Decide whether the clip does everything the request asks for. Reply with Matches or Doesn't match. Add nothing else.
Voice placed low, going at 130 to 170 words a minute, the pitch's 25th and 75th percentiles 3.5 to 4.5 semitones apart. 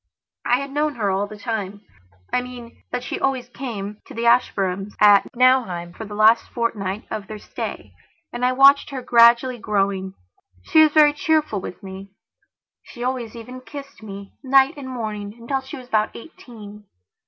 Doesn't match